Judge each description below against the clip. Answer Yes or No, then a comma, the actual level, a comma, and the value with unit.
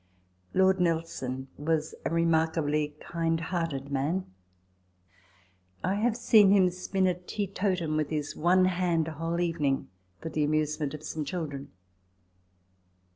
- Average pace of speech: No, slow, 130 wpm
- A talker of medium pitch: Yes, medium, 165 Hz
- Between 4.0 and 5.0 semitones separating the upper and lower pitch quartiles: No, average, 3.1 semitones